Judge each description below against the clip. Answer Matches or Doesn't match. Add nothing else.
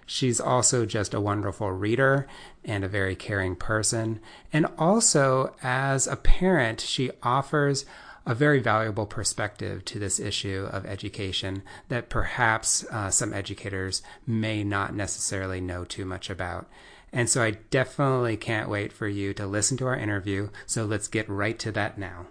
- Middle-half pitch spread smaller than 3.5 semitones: Doesn't match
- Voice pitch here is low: Matches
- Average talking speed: Matches